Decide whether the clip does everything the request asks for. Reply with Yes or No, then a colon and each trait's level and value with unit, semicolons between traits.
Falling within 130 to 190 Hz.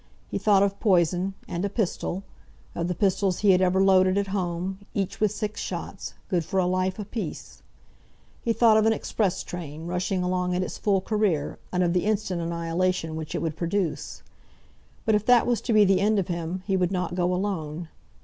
Yes: medium, 185 Hz